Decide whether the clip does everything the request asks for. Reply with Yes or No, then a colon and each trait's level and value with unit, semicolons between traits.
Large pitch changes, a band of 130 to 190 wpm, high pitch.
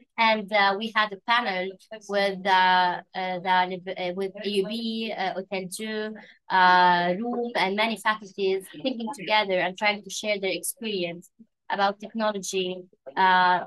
No: average, 2.7 semitones; slow, 135 wpm; high, 195 Hz